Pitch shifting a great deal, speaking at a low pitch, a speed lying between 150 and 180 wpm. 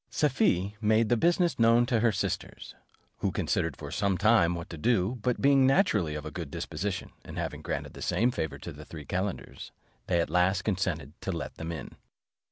No: wide, 5.8 semitones; low, 100 Hz; average, 195 wpm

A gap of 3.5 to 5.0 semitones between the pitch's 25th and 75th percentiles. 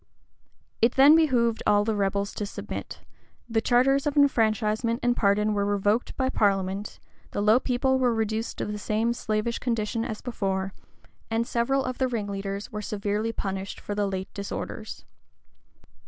No: average, 3.0 semitones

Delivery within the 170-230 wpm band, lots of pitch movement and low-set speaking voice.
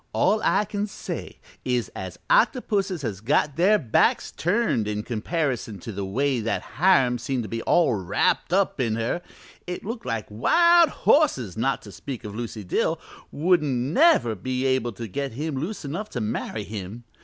Yes: average, 175 wpm; wide, 8.2 semitones; low, 130 Hz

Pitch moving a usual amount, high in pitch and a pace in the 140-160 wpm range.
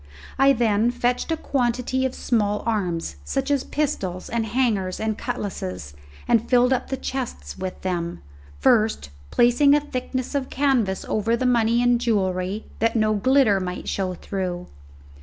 Yes: average, 5.0 semitones; high, 230 Hz; average, 155 wpm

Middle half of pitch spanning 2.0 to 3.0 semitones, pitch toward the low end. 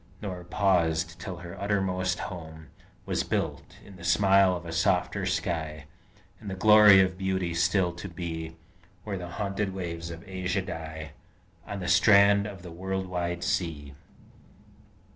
Yes: narrow, 2.5 semitones; very low, 90 Hz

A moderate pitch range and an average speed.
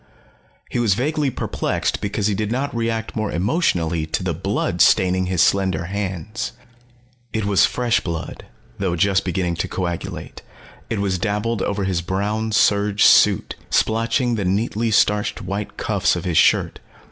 Yes: average, 3.2 semitones; average, 155 wpm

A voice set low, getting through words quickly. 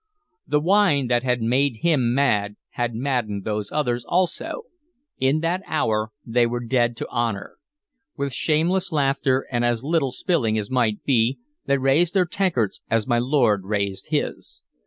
No: low, 125 Hz; average, 155 wpm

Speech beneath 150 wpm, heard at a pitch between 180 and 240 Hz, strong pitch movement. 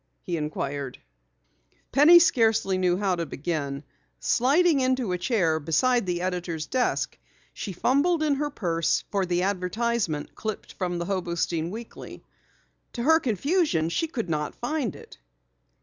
Yes: average, 140 wpm; high, 190 Hz; wide, 7.2 semitones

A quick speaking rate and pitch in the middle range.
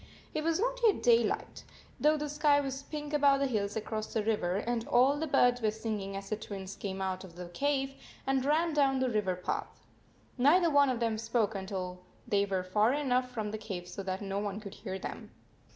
No: fast, 215 wpm; high, 225 Hz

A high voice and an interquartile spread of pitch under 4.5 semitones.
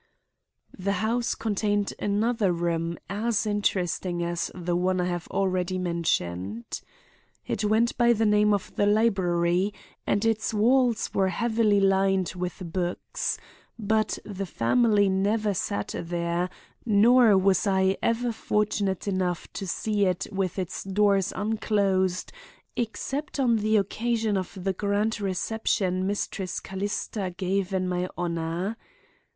Yes: high, 195 Hz; average, 2.9 semitones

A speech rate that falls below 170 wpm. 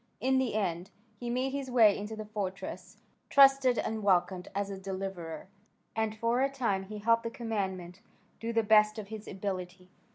No: average, 175 wpm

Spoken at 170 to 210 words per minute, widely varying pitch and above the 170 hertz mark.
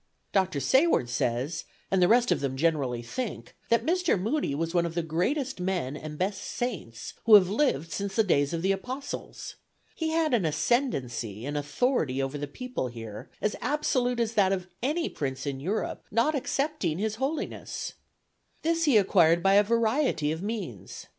Yes: average, 175 wpm; wide, 9.0 semitones; high, 190 Hz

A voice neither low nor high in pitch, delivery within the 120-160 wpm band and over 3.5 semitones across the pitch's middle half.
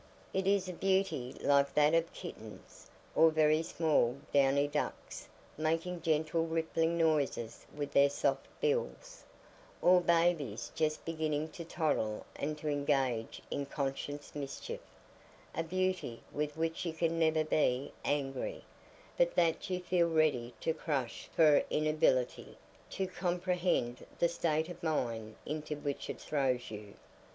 No: medium, 155 Hz; slow, 135 wpm; average, 3.0 semitones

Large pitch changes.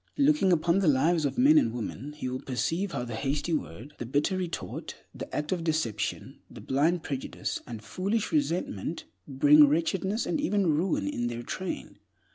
Yes: wide, 6.2 semitones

